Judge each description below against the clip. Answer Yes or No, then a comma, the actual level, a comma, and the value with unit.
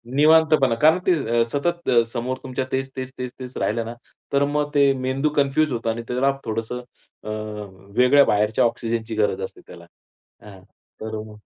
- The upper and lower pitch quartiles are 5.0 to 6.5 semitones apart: No, average, 3.6 semitones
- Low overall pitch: Yes, low, 130 Hz